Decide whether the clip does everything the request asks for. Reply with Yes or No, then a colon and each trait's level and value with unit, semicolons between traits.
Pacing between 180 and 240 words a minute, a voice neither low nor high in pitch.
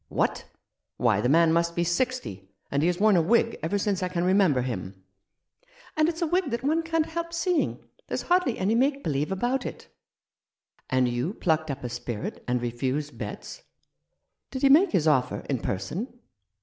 Yes: average, 190 wpm; medium, 180 Hz